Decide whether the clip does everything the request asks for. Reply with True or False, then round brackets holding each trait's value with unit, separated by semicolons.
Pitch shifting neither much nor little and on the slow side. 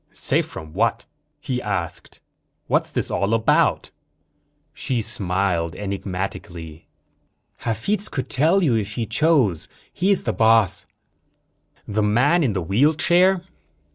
False (7.3 semitones; 115 wpm)